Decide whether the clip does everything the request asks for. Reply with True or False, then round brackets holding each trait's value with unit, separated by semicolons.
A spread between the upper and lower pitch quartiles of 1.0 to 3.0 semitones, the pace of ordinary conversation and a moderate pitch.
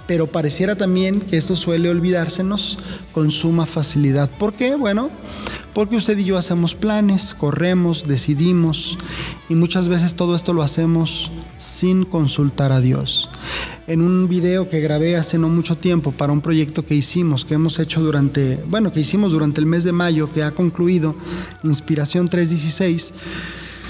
True (2.5 semitones; 160 wpm; 170 Hz)